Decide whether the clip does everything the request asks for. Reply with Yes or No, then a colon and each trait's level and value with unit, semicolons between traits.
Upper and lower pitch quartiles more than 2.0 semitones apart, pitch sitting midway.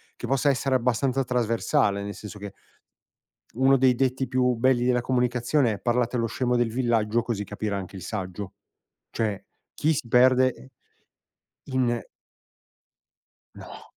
No: average, 2.7 semitones; low, 125 Hz